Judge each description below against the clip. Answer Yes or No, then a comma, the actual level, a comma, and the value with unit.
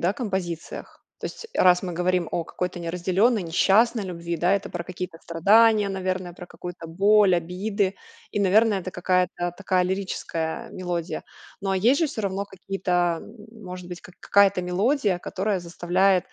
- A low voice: No, medium, 185 Hz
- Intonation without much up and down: Yes, narrow, 2.3 semitones